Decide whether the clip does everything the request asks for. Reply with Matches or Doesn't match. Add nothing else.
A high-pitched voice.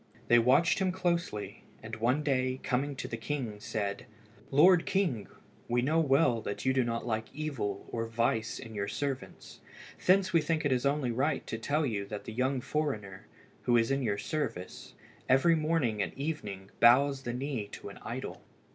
Doesn't match